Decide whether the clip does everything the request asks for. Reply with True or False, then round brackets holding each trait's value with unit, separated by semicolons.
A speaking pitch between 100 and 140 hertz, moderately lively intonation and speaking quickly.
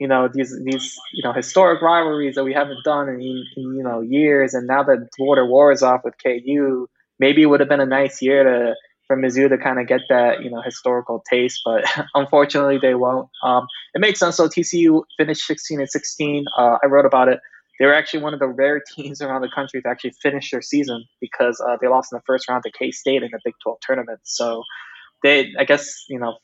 False (135 Hz; 2.2 semitones; 235 wpm)